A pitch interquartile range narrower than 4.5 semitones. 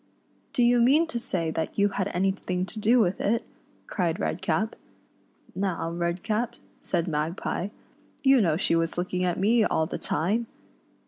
No: average, 4.8 semitones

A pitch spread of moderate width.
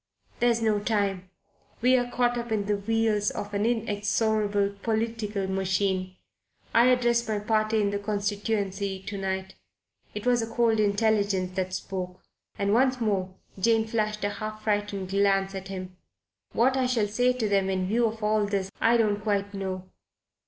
No: narrow, 2.3 semitones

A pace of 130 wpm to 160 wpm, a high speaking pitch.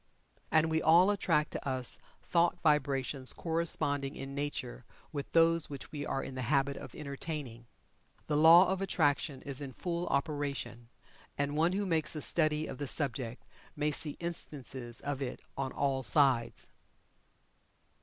No: average, 155 wpm; medium, 145 Hz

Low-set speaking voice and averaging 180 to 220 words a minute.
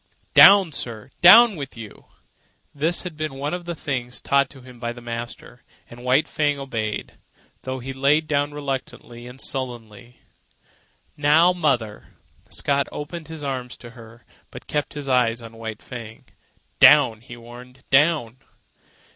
No: low, 130 Hz; average, 145 wpm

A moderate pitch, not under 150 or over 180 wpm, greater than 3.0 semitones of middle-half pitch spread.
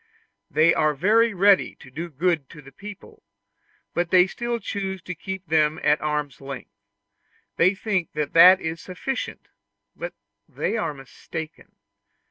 No: medium, 170 Hz; average, 140 wpm; average, 4.4 semitones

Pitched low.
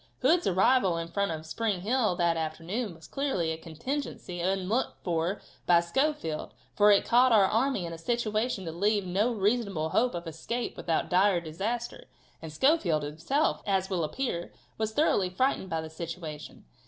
No: high, 190 Hz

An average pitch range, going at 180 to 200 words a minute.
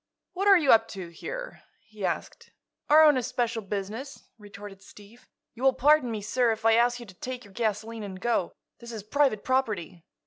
Yes: average, 3.9 semitones; average, 195 wpm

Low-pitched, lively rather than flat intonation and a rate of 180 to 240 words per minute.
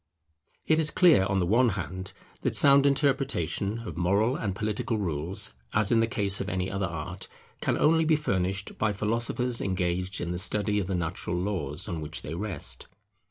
No: low, 100 Hz; average, 4.4 semitones; average, 185 wpm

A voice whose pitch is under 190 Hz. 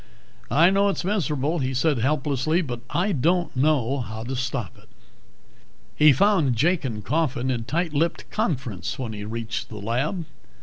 Yes: medium, 140 Hz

